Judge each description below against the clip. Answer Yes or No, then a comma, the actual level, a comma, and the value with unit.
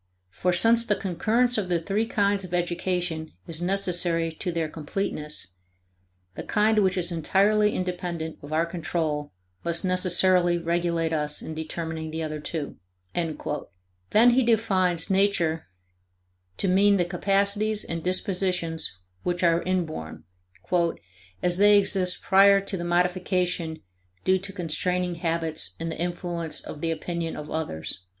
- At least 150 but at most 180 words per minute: No, average, 140 wpm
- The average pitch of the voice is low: No, medium, 175 Hz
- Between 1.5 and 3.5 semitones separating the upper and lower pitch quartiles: Yes, average, 3.0 semitones